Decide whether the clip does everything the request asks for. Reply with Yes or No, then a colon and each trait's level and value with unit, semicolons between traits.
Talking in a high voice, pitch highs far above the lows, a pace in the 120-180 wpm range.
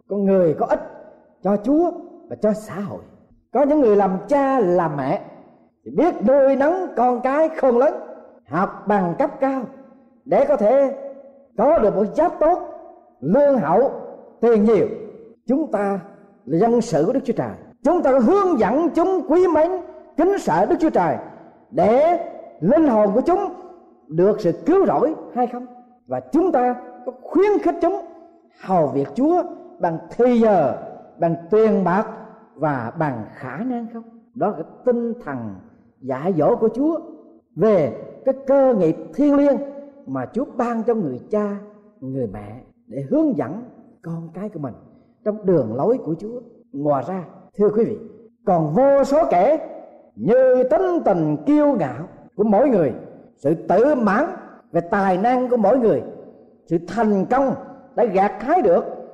Yes: very high, 250 Hz; wide, 6.7 semitones; slow, 165 wpm